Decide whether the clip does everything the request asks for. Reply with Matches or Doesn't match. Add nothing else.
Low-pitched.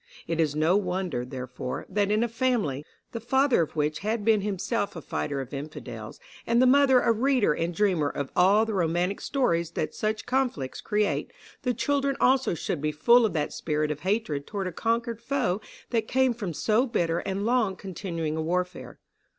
Doesn't match